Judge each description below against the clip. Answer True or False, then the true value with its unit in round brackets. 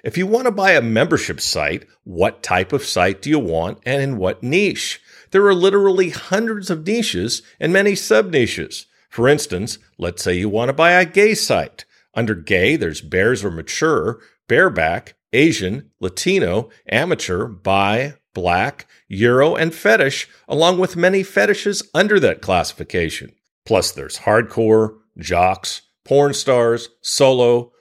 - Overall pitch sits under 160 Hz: True (140 Hz)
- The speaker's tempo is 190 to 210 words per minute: False (150 wpm)